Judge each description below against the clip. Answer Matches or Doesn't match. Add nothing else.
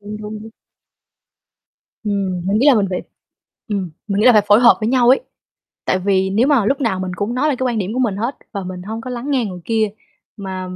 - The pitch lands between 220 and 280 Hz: Doesn't match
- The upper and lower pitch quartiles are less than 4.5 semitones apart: Matches